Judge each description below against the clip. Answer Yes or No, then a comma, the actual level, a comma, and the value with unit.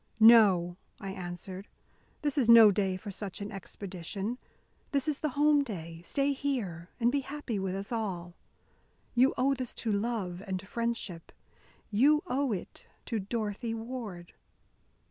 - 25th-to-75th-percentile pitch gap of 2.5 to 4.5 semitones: No, average, 5.1 semitones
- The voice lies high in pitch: Yes, high, 215 Hz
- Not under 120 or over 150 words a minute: Yes, average, 145 wpm